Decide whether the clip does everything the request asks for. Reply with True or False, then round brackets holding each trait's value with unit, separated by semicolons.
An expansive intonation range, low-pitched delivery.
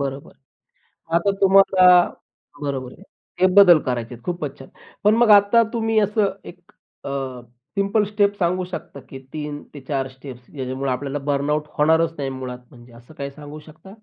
False (6.4 semitones; 150 Hz)